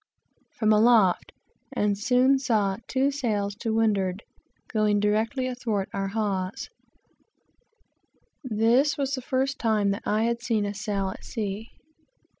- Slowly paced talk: Yes, slow, 130 wpm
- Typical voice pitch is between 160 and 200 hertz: No, high, 220 Hz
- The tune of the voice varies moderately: Yes, average, 3.5 semitones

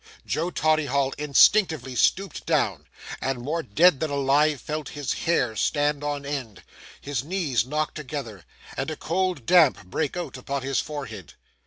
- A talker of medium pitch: Yes, medium, 145 Hz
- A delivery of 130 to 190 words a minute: Yes, average, 150 wpm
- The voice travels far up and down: No, average, 3.1 semitones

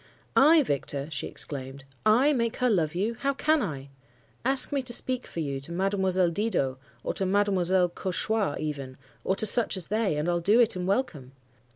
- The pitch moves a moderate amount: No, wide, 6.9 semitones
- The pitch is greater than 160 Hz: Yes, high, 190 Hz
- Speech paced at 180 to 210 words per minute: Yes, average, 190 wpm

